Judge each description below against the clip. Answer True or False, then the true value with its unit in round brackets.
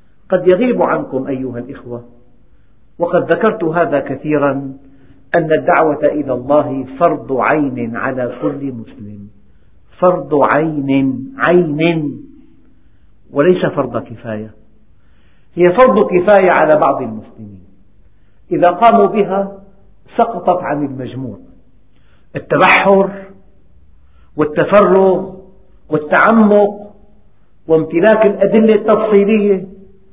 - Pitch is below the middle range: False (150 Hz)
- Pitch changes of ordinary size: False (7.7 semitones)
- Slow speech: False (85 wpm)